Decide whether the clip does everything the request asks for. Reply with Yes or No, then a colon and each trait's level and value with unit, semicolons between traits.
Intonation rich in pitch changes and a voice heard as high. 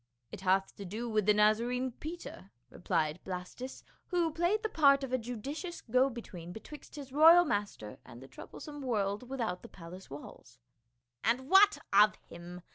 Yes: wide, 7.4 semitones; high, 220 Hz